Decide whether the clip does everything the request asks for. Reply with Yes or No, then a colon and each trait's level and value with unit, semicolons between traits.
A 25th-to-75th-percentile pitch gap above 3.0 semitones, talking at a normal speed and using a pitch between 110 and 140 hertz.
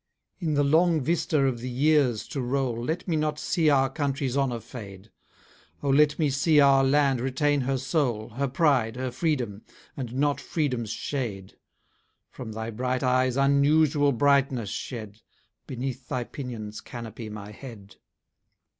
Yes: average, 3.4 semitones; average, 150 wpm; low, 135 Hz